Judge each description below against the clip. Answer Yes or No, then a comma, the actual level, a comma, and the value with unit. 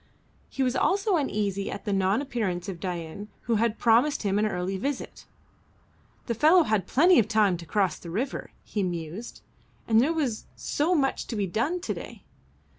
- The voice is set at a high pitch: Yes, high, 215 Hz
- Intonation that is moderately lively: No, wide, 5.9 semitones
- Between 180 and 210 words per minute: Yes, average, 185 wpm